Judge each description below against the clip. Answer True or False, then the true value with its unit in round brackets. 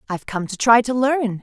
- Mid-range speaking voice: False (230 Hz)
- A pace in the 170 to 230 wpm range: False (255 wpm)